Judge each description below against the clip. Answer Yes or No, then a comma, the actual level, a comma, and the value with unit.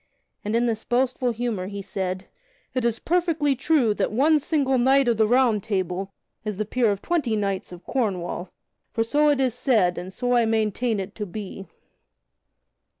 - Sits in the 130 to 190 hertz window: No, high, 225 Hz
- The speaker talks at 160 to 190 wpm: Yes, average, 180 wpm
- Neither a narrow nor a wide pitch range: Yes, average, 4.6 semitones